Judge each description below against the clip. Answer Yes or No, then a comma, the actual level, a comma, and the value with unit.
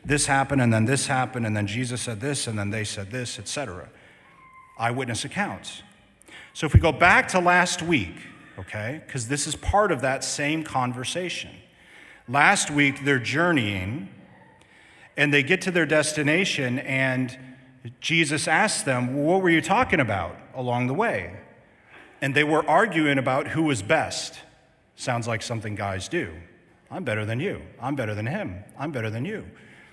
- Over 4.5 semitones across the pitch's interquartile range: Yes, average, 5.1 semitones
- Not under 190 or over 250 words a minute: No, average, 170 wpm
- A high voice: No, low, 135 Hz